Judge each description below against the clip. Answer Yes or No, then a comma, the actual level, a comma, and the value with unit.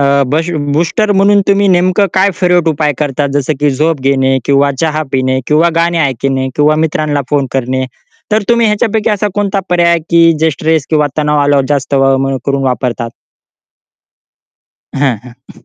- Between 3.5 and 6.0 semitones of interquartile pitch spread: Yes, average, 4.3 semitones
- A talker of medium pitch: Yes, medium, 150 Hz